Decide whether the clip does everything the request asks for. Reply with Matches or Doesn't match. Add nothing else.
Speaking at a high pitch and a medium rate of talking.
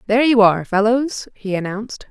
Matches